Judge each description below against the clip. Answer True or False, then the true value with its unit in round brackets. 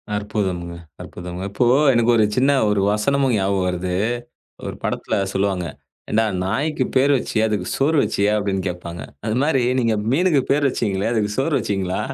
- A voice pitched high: False (105 Hz)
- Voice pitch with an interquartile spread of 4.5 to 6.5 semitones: True (5.3 semitones)